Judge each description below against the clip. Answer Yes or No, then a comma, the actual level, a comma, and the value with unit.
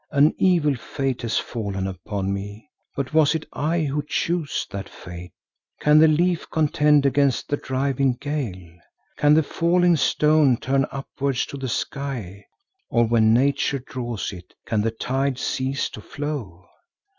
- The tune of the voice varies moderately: Yes, average, 4.9 semitones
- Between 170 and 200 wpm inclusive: No, average, 150 wpm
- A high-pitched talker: No, low, 135 Hz